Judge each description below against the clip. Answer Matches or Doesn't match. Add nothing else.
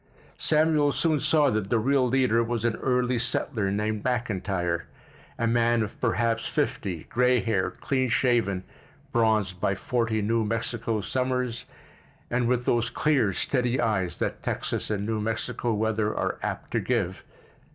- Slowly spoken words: Doesn't match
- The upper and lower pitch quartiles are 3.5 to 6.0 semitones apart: Doesn't match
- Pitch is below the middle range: Matches